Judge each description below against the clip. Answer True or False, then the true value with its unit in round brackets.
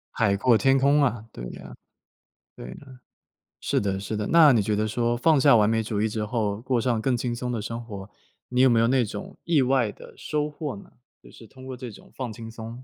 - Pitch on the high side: False (120 Hz)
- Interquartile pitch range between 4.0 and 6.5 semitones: False (3.5 semitones)